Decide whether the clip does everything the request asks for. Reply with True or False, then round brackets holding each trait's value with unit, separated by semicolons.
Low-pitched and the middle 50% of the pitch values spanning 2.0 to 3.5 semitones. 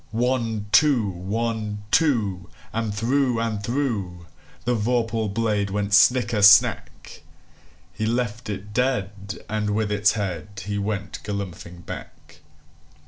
True (105 Hz; 2.4 semitones)